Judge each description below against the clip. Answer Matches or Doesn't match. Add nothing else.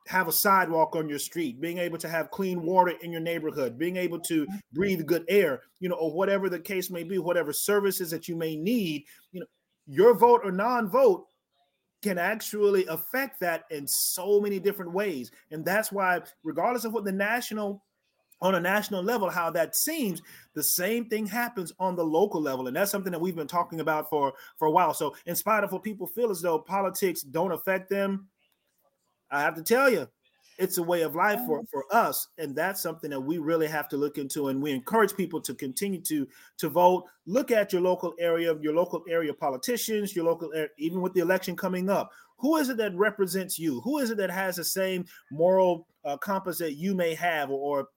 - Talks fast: Matches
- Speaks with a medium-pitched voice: Matches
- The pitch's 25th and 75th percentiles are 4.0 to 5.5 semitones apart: Doesn't match